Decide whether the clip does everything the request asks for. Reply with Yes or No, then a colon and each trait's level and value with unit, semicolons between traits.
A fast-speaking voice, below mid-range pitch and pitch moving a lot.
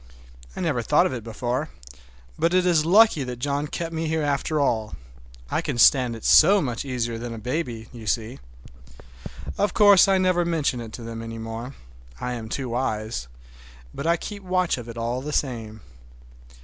No: average, 180 wpm; low, 125 Hz; wide, 6.1 semitones